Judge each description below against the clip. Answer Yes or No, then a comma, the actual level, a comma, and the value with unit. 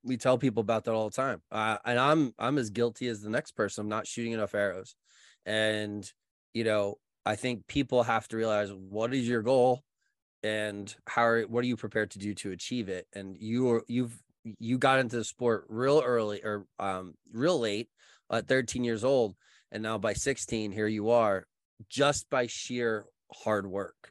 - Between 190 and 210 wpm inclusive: Yes, average, 200 wpm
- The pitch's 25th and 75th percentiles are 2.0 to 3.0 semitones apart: Yes, average, 2.7 semitones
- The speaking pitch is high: No, low, 115 Hz